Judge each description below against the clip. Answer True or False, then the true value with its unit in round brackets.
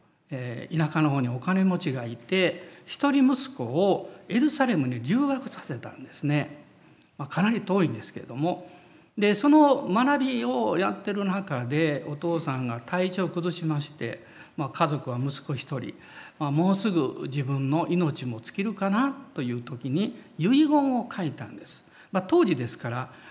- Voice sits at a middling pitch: True (175 Hz)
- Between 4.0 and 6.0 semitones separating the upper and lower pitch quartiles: False (6.5 semitones)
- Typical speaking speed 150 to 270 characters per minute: False (305 characters per minute)